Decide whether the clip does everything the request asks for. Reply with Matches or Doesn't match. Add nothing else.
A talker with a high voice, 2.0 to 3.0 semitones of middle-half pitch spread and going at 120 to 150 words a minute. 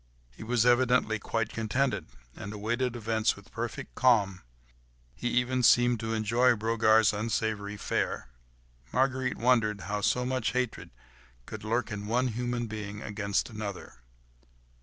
Doesn't match